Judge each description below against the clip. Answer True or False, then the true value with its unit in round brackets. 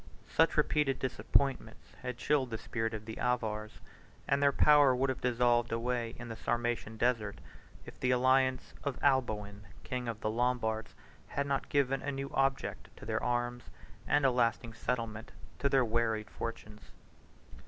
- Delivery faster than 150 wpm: True (165 wpm)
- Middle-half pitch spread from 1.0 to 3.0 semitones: True (2.7 semitones)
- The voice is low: True (120 Hz)